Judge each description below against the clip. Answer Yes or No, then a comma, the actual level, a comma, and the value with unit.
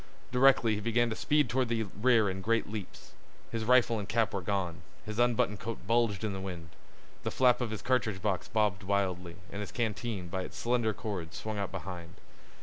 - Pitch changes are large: No, average, 3.5 semitones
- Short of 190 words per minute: No, average, 200 wpm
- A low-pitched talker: Yes, low, 110 Hz